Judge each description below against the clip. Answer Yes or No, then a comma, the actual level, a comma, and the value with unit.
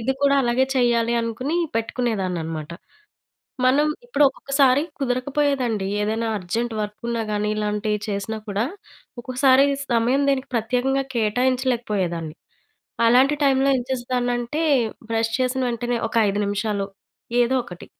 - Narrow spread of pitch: No, average, 3.6 semitones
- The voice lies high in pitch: Yes, high, 240 Hz